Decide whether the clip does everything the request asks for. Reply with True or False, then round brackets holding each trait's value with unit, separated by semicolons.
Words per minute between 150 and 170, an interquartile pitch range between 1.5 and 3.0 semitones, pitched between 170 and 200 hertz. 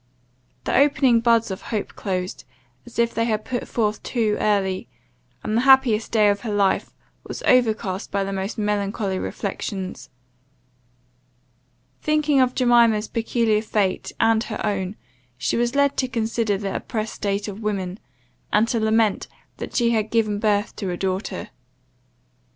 False (155 wpm; 2.6 semitones; 215 Hz)